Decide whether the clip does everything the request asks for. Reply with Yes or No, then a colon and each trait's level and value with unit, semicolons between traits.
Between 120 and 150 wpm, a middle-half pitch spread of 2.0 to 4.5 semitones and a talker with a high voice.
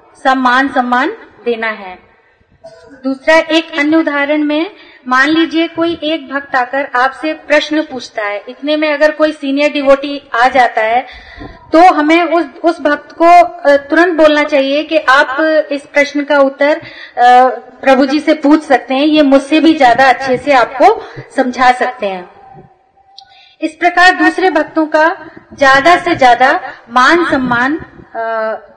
Yes: average, 145 wpm; average, 3.8 semitones; very high, 295 Hz